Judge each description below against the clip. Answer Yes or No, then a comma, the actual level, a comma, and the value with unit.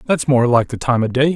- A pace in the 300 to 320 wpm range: Yes, fast, 310 wpm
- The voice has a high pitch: No, low, 130 Hz